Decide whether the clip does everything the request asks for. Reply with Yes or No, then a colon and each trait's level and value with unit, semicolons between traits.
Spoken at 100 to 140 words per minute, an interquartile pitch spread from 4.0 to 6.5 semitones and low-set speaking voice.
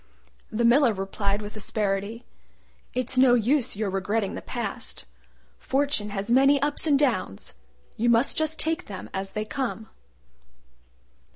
No: slow, 135 wpm; average, 5.0 semitones; high, 230 Hz